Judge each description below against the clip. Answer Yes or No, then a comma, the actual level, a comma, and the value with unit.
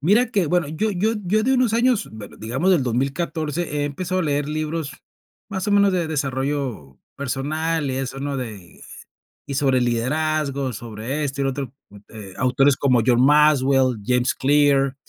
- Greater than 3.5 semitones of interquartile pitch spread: Yes, average, 4.1 semitones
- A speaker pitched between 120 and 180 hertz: Yes, medium, 140 Hz